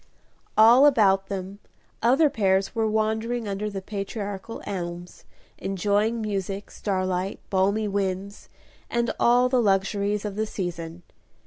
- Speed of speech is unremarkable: No, slow, 120 wpm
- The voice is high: Yes, high, 200 Hz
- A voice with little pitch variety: Yes, narrow, 2.3 semitones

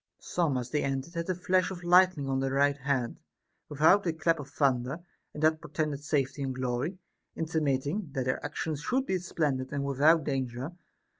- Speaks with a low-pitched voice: No, medium, 150 Hz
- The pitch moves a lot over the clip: No, average, 3.8 semitones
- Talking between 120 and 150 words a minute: No, average, 180 wpm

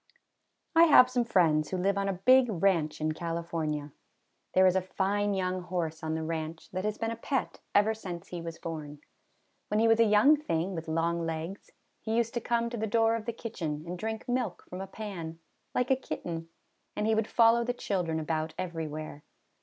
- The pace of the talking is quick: Yes, fast, 210 wpm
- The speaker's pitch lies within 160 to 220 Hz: Yes, medium, 185 Hz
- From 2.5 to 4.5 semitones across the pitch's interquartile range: No, average, 5.3 semitones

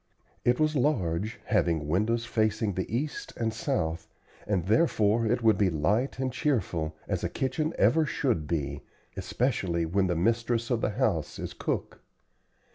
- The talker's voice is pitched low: Yes, low, 110 Hz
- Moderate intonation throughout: No, wide, 6.3 semitones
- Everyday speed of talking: Yes, average, 155 wpm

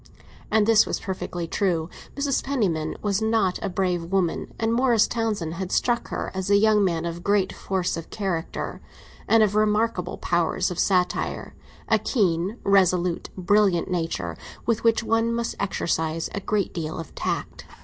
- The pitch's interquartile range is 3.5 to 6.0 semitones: Yes, average, 4.0 semitones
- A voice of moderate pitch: No, high, 195 Hz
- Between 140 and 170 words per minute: Yes, average, 160 wpm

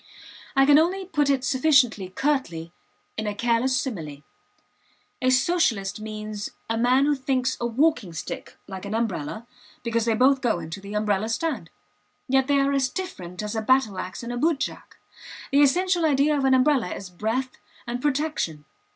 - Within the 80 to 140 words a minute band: No, average, 170 wpm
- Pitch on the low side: No, very high, 250 Hz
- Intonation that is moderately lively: Yes, average, 4.9 semitones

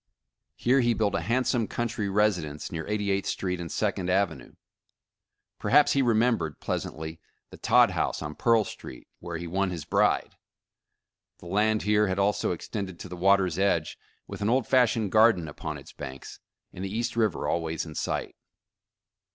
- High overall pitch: No, low, 100 Hz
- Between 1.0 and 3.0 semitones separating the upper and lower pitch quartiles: No, average, 4.3 semitones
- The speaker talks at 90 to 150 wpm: No, average, 170 wpm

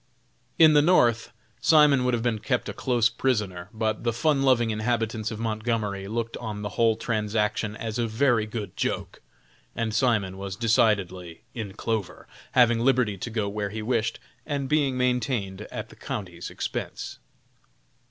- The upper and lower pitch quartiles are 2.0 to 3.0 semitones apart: Yes, narrow, 2.5 semitones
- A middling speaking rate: Yes, average, 160 wpm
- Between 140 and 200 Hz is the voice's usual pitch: No, low, 115 Hz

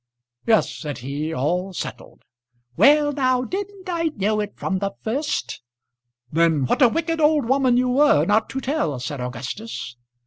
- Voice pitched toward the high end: Yes, high, 225 Hz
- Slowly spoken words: No, average, 160 wpm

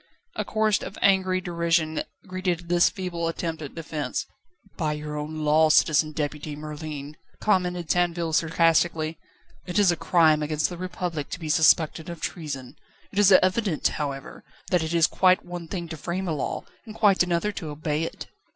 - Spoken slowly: No, average, 170 wpm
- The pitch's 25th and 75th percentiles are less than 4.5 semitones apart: Yes, average, 2.8 semitones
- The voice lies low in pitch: No, medium, 165 Hz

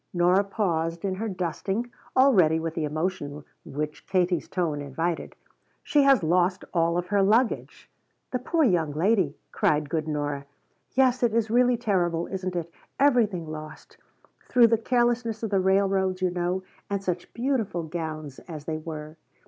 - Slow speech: No, average, 160 wpm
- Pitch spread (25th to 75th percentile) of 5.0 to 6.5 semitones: Yes, wide, 5.4 semitones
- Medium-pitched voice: Yes, medium, 180 Hz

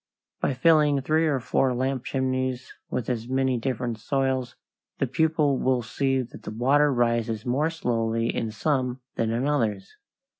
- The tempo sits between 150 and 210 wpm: Yes, average, 155 wpm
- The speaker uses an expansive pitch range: No, average, 2.7 semitones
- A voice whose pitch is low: Yes, low, 130 Hz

